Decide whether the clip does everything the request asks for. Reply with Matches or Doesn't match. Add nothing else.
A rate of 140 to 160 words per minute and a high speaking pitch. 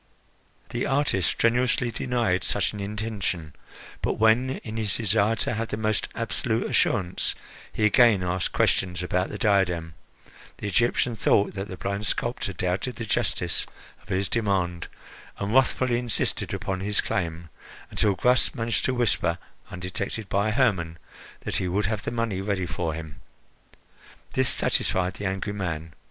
Doesn't match